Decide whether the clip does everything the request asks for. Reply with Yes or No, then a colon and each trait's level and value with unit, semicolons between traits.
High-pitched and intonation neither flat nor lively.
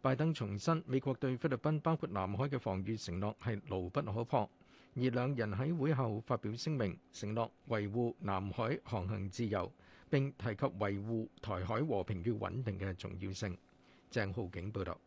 No: low, 110 Hz; average, 4.8 semitones